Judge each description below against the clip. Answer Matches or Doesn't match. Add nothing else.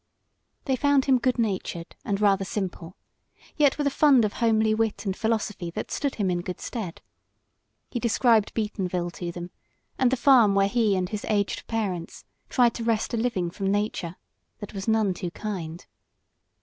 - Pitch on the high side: Matches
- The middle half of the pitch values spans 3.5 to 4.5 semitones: Matches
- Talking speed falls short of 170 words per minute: Doesn't match